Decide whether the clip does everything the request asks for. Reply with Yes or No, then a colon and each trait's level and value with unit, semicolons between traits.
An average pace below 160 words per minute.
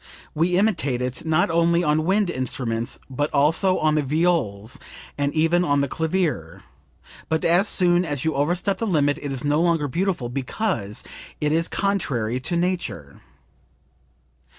Yes: average, 150 wpm